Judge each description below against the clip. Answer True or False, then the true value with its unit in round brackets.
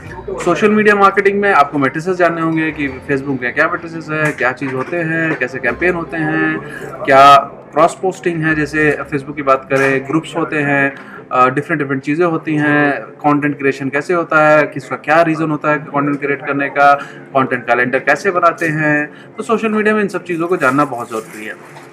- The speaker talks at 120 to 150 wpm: False (190 wpm)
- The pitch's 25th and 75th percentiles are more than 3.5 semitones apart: False (3.2 semitones)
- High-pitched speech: False (150 Hz)